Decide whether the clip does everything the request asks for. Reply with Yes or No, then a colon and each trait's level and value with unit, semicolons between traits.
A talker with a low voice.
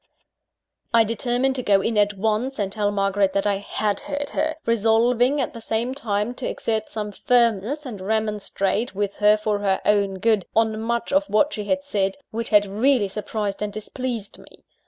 No: high, 215 Hz